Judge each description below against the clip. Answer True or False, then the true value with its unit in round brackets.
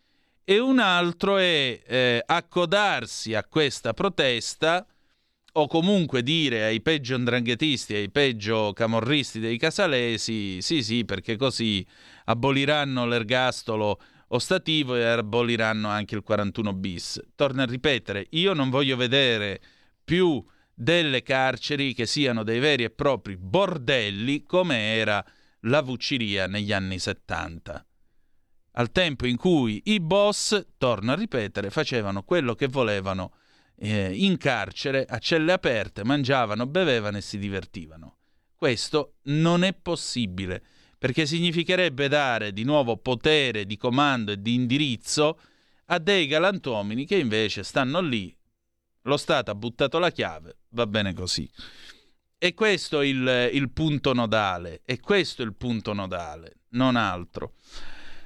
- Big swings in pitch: True (6.3 semitones)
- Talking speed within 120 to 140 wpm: True (130 wpm)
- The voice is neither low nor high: False (125 Hz)